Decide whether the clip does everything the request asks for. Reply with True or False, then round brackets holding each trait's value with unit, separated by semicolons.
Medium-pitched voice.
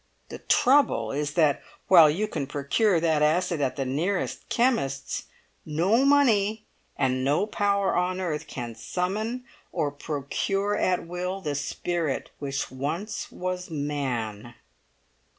True (165 Hz)